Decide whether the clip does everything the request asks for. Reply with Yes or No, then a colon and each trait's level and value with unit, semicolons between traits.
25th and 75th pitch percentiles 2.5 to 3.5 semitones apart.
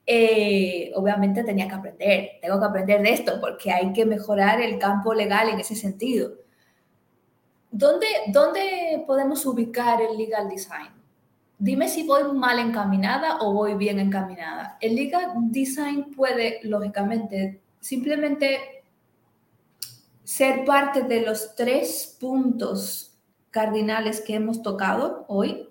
No: average, 4.6 semitones